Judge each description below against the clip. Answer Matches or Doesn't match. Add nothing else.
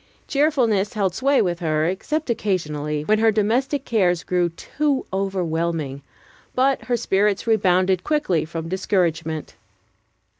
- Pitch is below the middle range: Doesn't match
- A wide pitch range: Matches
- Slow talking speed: Matches